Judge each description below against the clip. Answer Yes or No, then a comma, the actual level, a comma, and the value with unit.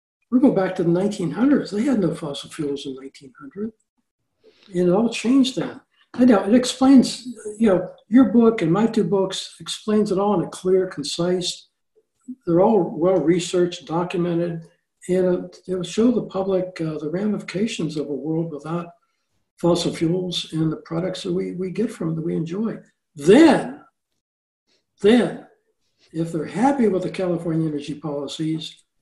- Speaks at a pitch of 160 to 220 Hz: Yes, medium, 185 Hz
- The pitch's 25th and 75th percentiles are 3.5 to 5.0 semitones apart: Yes, average, 4.7 semitones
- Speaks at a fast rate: No, average, 165 wpm